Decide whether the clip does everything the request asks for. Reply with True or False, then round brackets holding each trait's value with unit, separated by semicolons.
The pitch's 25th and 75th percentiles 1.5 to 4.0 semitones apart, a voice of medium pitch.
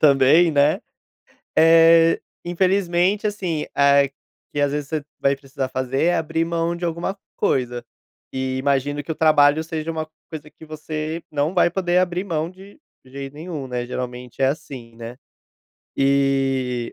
True (3.6 semitones; 150 Hz)